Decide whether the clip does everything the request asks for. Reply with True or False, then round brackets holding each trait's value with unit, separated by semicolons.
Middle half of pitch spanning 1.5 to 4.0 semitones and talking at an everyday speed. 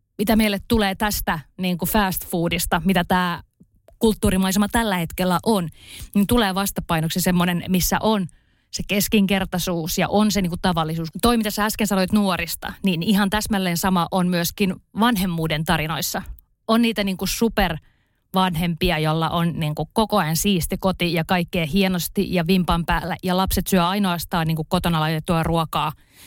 False (2.8 semitones; 160 wpm)